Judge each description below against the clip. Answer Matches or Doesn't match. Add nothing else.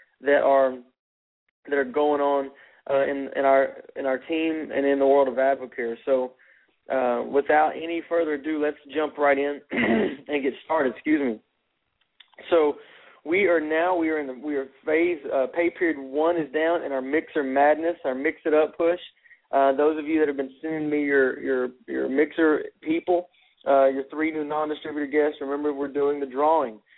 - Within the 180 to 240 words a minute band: Matches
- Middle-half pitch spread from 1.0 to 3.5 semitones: Matches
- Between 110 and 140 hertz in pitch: Doesn't match